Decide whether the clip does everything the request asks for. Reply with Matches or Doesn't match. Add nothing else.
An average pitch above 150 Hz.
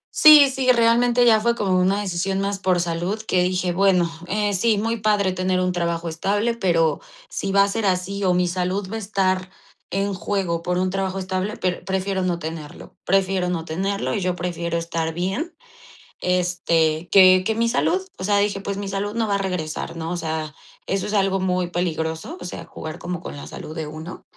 Matches